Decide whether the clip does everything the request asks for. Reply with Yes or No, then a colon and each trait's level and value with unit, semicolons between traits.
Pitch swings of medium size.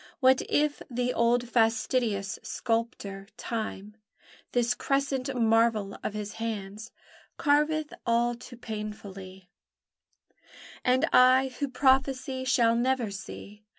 Yes: average, 3.4 semitones